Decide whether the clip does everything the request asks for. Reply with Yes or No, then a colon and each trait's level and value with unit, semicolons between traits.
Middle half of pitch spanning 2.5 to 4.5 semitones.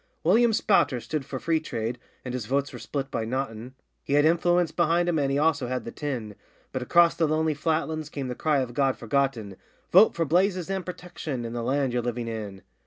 No: average, 5.0 semitones